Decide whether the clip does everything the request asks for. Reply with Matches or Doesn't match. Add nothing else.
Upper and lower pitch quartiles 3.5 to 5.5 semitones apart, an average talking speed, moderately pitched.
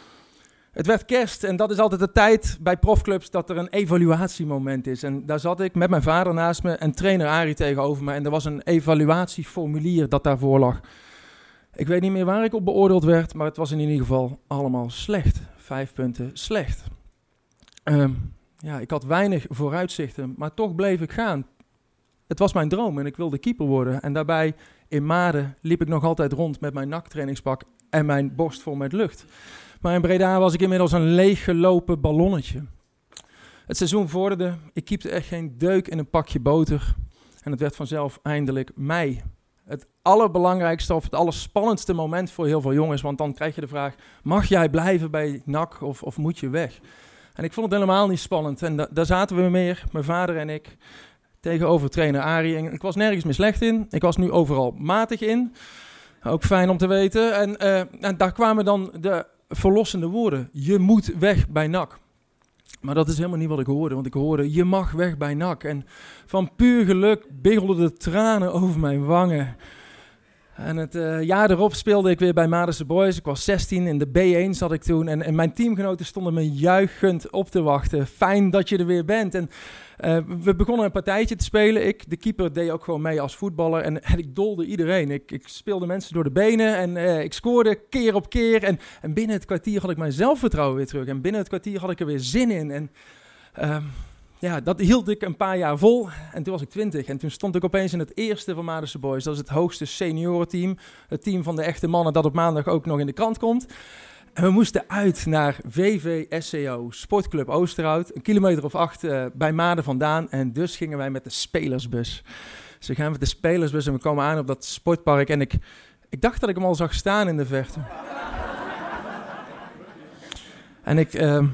Doesn't match